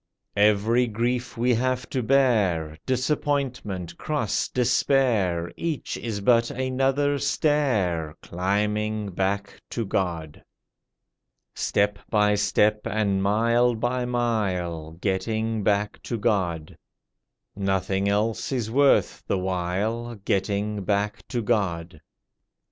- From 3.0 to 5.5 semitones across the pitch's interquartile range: Yes, average, 4.1 semitones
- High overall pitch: No, low, 105 Hz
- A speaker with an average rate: No, slow, 105 wpm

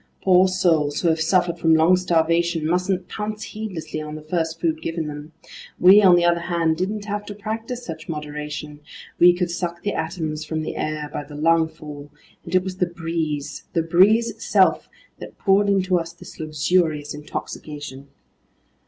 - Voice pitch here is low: No, medium, 165 Hz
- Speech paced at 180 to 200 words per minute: No, average, 170 wpm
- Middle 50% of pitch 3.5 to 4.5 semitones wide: No, average, 3.0 semitones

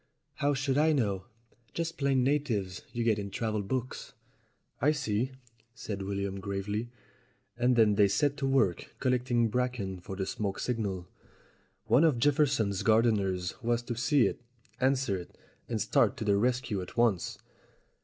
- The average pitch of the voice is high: No, low, 115 Hz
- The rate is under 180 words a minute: Yes, average, 155 wpm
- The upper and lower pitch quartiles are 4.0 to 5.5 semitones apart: Yes, average, 4.7 semitones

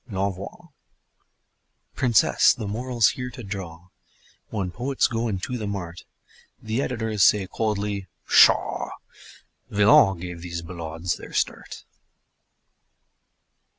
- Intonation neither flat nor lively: Yes, average, 3.7 semitones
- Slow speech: Yes, slow, 105 wpm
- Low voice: Yes, low, 100 Hz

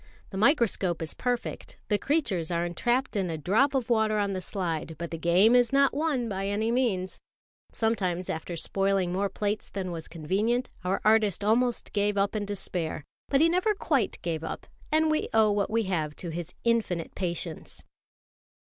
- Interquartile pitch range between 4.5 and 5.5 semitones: Yes, average, 5.1 semitones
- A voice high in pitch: Yes, high, 200 Hz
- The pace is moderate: Yes, average, 180 wpm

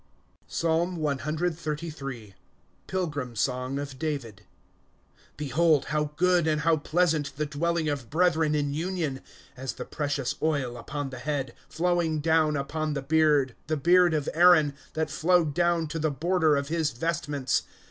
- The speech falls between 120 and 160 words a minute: Yes, average, 150 wpm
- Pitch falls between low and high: Yes, medium, 155 Hz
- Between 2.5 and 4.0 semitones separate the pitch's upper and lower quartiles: Yes, average, 2.8 semitones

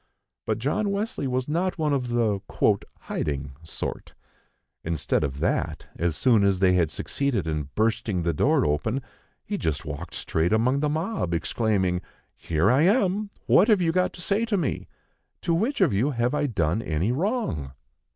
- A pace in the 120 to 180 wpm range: Yes, average, 170 wpm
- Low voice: Yes, low, 115 Hz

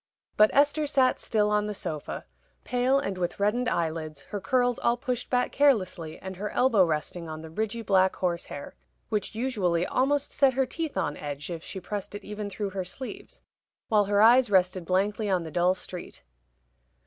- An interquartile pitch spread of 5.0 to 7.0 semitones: Yes, wide, 5.5 semitones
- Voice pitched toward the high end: Yes, high, 205 Hz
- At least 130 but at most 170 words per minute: No, average, 185 wpm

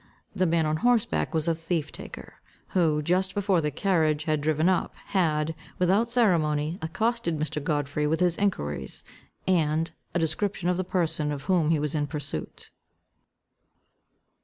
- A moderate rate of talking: Yes, average, 160 wpm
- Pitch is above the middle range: No, medium, 160 Hz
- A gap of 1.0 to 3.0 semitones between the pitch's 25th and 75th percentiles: No, average, 3.4 semitones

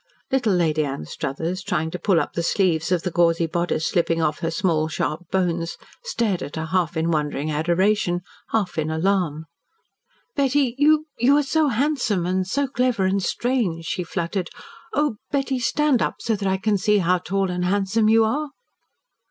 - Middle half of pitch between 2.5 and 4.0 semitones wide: No, average, 5.3 semitones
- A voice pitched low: No, medium, 185 Hz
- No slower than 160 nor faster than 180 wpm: Yes, average, 175 wpm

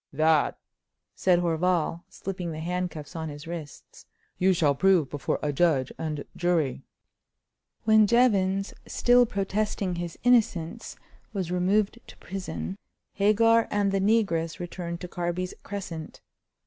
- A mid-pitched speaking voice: Yes, medium, 180 Hz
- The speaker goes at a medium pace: No, slow, 125 wpm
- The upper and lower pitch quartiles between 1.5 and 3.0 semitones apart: No, average, 3.5 semitones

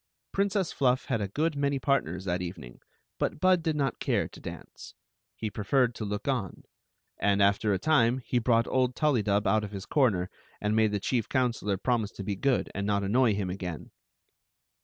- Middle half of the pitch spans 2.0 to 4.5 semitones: No, average, 4.9 semitones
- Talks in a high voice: No, low, 110 Hz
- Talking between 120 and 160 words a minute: No, average, 200 wpm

